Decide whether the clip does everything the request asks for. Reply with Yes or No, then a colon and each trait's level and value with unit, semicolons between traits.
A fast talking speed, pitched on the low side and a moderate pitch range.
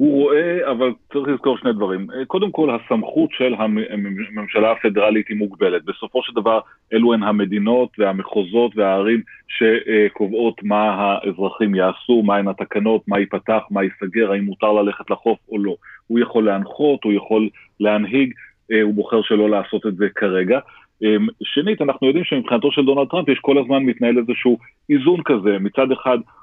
Yes: fast, 155 wpm; low, 110 Hz; average, 3.7 semitones